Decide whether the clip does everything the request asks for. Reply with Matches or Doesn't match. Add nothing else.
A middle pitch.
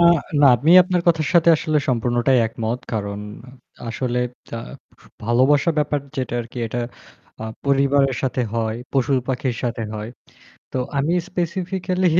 Doesn't match